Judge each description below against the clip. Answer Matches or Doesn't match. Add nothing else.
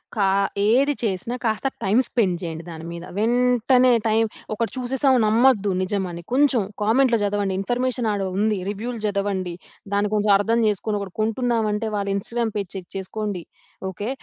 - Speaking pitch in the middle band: Doesn't match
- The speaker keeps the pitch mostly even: Doesn't match